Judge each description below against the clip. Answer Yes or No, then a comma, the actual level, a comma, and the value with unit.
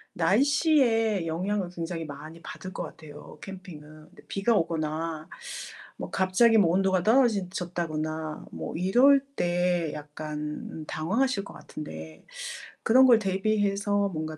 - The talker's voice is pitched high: No, medium, 180 Hz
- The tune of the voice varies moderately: Yes, average, 4.6 semitones